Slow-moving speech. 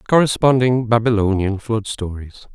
Yes: slow, 120 wpm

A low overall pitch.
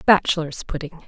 No: medium, 160 Hz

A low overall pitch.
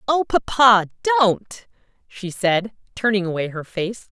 No: high, 210 Hz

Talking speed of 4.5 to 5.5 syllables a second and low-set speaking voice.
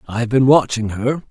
Yes: 5.3 syllables/s; low, 120 Hz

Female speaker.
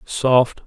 No: male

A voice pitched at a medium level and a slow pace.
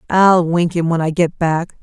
No: medium, 170 Hz; fast, 230 wpm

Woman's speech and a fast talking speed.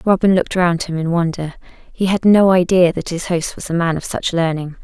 Yes: female; fast, 235 wpm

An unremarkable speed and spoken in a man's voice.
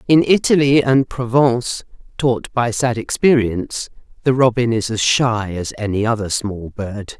No: average, 150 wpm; female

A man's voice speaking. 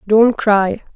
No: female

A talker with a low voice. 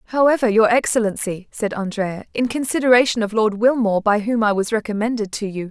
No: high, 220 Hz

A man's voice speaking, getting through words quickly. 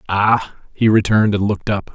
No: male; average, 185 wpm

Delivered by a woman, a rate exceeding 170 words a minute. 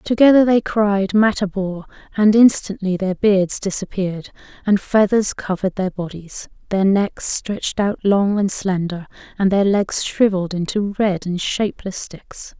No: female; average, 145 wpm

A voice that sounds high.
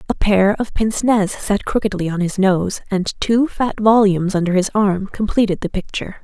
Yes: high, 200 Hz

